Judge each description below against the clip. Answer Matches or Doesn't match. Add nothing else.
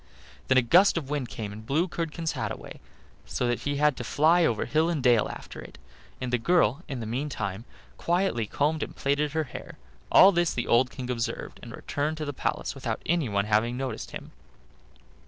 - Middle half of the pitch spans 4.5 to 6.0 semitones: Matches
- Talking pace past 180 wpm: Matches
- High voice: Doesn't match